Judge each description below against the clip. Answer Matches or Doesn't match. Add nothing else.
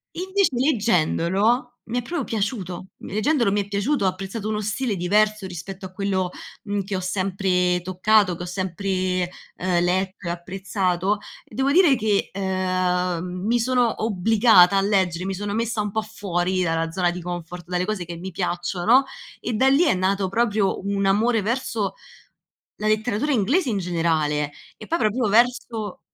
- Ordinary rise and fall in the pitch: Matches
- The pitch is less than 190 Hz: Doesn't match